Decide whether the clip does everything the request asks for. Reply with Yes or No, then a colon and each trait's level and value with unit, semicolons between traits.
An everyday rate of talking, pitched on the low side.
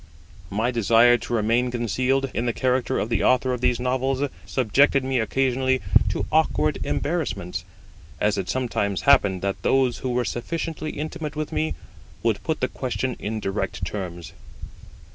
Yes: average, 155 wpm; low, 125 Hz